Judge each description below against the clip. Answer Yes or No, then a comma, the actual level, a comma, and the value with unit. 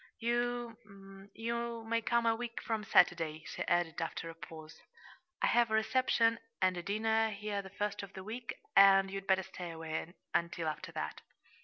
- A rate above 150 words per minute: Yes, average, 175 wpm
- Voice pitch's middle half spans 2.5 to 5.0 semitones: Yes, average, 4.4 semitones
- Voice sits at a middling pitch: No, high, 200 Hz